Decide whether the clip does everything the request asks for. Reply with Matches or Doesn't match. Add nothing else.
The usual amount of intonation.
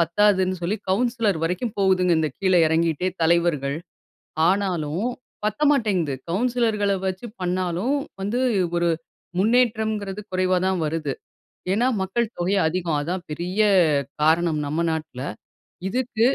Matches